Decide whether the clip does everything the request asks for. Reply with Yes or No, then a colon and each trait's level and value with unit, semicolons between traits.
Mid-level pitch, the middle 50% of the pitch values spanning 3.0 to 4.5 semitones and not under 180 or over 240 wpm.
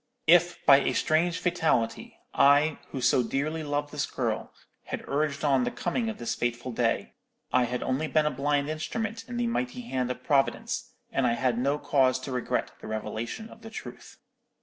No: medium, 145 Hz; average, 5.2 semitones; average, 190 wpm